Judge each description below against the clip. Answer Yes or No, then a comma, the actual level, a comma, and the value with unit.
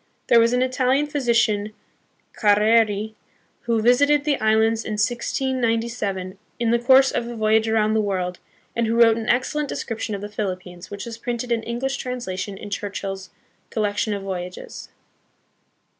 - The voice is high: Yes, high, 225 Hz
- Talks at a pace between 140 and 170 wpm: Yes, average, 155 wpm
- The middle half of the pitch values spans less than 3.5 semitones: Yes, average, 2.8 semitones